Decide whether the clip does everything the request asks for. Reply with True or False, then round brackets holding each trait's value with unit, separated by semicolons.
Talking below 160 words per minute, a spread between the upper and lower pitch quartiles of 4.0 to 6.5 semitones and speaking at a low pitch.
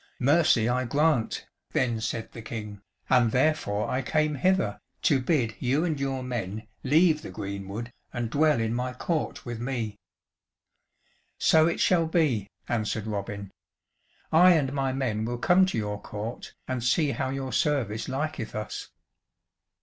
True (150 wpm; 5.2 semitones; 125 Hz)